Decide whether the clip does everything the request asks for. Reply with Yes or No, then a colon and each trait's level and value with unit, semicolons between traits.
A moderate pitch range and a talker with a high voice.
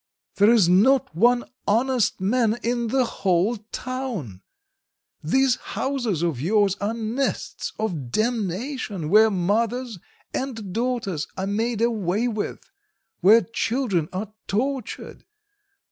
Yes: average, 4.3 semitones; high, 220 Hz